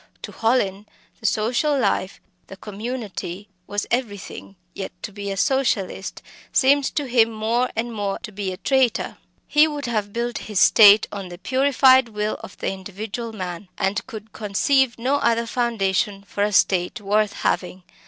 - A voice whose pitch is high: Yes, high, 215 Hz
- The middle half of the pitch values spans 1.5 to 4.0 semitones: Yes, average, 3.5 semitones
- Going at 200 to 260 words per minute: No, average, 165 wpm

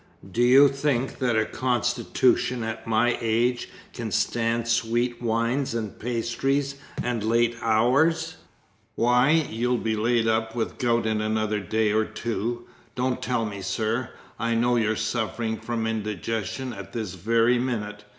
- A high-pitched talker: No, low, 115 Hz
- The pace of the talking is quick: No, average, 145 wpm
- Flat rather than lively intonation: Yes, narrow, 1.8 semitones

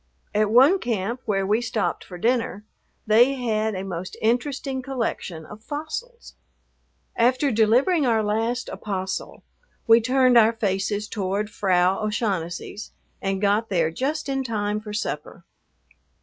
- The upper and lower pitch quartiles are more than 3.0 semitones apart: Yes, average, 3.9 semitones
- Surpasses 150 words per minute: No, slow, 135 wpm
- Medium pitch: No, high, 220 Hz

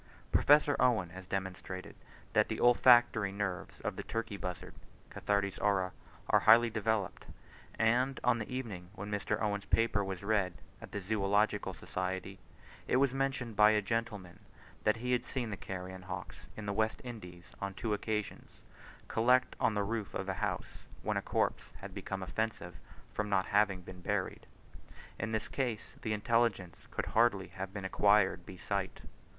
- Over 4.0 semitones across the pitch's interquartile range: No, average, 3.2 semitones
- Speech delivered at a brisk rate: No, average, 165 wpm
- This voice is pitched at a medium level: No, low, 105 Hz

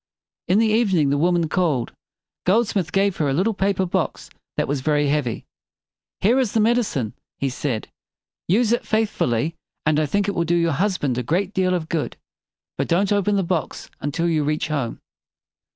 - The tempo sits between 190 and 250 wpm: Yes, average, 200 wpm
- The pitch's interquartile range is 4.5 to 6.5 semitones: Yes, average, 5.3 semitones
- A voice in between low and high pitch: Yes, medium, 170 Hz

